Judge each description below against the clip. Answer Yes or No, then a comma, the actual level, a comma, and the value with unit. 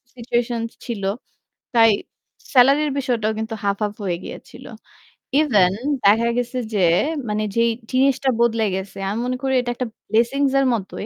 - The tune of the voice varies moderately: Yes, average, 3.2 semitones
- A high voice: Yes, high, 235 Hz